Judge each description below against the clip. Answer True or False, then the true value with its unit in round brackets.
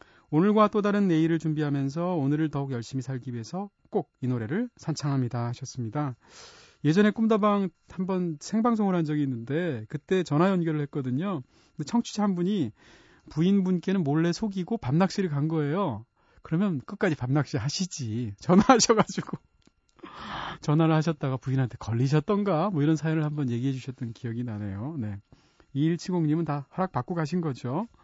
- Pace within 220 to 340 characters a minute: False (350 characters per minute)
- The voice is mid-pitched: True (155 Hz)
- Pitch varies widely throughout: True (5.8 semitones)